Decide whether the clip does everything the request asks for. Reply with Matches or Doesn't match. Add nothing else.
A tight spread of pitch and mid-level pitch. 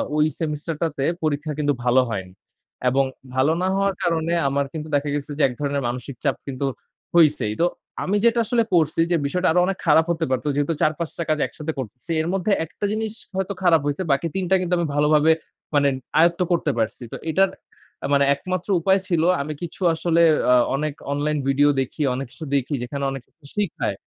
Doesn't match